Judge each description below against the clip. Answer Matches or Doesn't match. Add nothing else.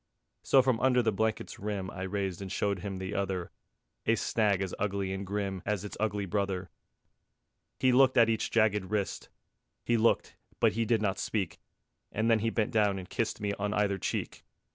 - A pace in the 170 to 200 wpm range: Matches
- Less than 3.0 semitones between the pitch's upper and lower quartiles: Matches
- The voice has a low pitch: Matches